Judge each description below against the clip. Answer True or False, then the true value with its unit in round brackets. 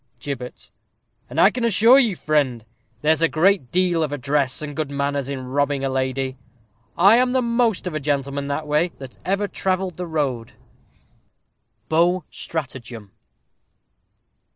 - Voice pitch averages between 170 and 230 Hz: False (150 Hz)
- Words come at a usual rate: True (150 wpm)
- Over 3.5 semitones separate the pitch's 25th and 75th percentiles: True (5.1 semitones)